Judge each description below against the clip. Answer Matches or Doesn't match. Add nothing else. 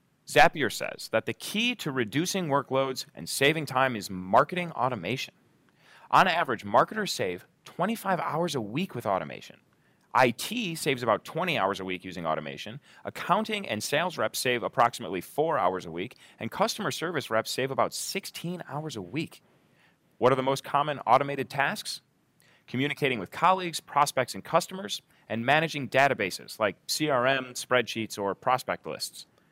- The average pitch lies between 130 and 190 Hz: Matches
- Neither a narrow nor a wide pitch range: Doesn't match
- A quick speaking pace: Doesn't match